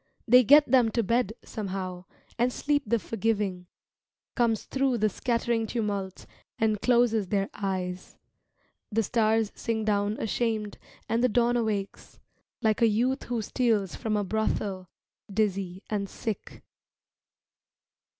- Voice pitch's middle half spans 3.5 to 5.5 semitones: No, average, 2.9 semitones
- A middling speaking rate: No, slow, 130 wpm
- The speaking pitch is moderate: No, high, 220 Hz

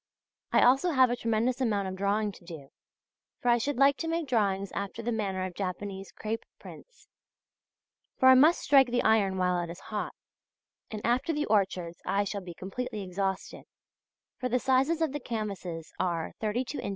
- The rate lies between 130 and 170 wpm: No, average, 185 wpm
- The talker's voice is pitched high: Yes, high, 215 Hz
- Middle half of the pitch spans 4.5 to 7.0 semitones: Yes, average, 5.0 semitones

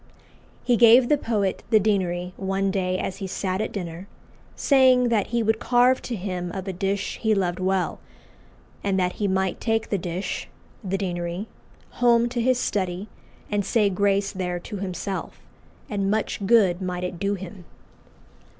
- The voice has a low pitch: No, high, 195 Hz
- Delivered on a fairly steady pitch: No, average, 3.1 semitones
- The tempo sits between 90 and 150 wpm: No, average, 170 wpm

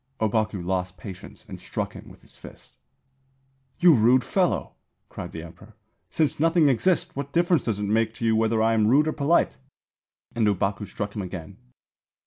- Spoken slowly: No, average, 175 wpm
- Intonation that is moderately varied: No, wide, 6.1 semitones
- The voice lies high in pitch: No, low, 110 Hz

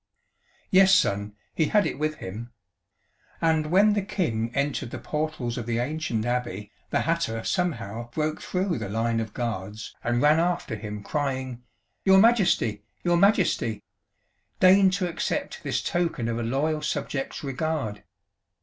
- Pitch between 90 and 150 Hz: Yes, medium, 140 Hz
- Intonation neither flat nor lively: No, wide, 7.0 semitones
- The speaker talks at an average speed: Yes, average, 150 wpm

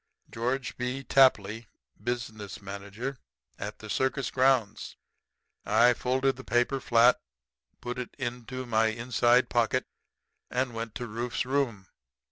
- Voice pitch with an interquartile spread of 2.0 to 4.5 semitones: Yes, narrow, 2.5 semitones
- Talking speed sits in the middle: No, slow, 125 wpm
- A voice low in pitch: Yes, low, 120 Hz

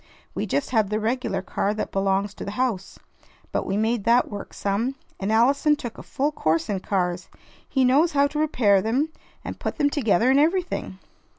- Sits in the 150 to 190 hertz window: No, high, 225 Hz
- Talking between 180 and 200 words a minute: Yes, average, 195 wpm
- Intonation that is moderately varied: No, wide, 5.8 semitones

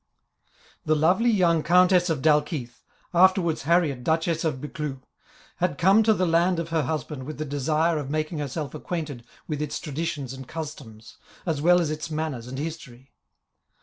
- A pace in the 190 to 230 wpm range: No, average, 165 wpm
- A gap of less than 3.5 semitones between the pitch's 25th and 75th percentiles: Yes, average, 3.0 semitones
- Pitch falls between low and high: Yes, medium, 155 Hz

